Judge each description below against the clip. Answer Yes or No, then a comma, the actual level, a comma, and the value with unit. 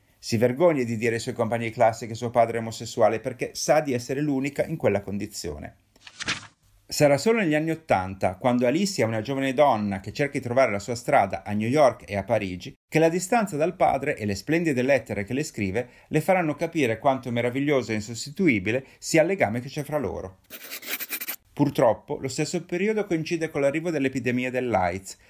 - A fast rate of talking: Yes, fast, 190 wpm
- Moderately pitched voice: No, low, 125 Hz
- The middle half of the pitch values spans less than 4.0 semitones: No, average, 5.3 semitones